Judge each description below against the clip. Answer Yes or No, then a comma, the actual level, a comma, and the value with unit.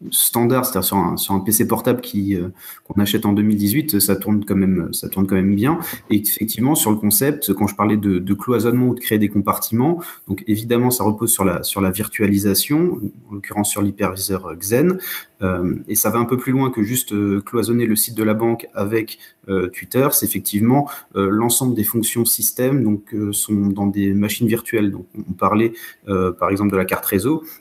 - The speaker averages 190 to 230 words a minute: Yes, average, 215 wpm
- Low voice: Yes, low, 105 Hz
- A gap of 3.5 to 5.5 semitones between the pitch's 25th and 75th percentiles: No, average, 2.9 semitones